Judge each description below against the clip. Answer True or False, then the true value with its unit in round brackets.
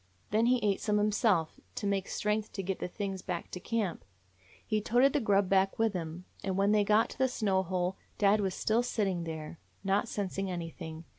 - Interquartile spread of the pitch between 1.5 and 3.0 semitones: True (2.6 semitones)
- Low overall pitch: False (195 Hz)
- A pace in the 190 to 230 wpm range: True (205 wpm)